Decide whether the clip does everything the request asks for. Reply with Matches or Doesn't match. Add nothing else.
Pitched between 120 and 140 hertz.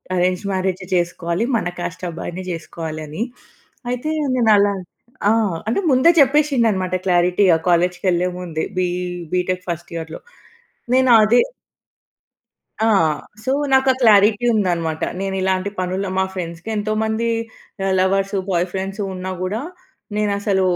Doesn't match